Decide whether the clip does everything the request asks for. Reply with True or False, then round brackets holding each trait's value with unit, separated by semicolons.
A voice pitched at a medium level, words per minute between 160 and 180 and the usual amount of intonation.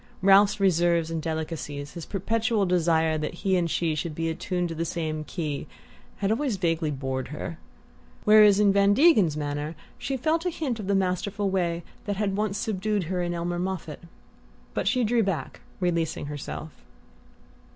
True (175 Hz; 170 wpm; 4.0 semitones)